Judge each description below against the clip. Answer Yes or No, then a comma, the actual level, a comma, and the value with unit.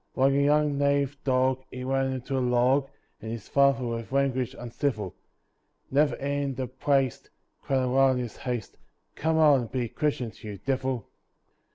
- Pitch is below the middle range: Yes, low, 130 Hz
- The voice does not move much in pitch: Yes, narrow, 2.0 semitones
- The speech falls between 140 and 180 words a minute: Yes, average, 165 wpm